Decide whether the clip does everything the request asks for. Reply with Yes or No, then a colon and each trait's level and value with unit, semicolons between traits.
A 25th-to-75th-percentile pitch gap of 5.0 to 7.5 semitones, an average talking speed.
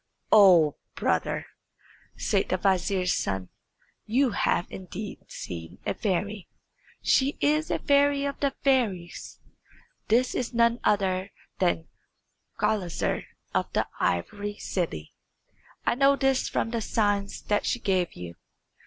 No: wide, 5.6 semitones; slow, 125 wpm